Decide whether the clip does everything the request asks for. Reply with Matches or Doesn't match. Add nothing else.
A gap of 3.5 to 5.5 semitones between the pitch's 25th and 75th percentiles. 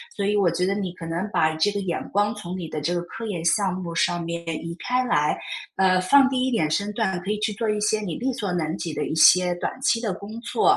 Matches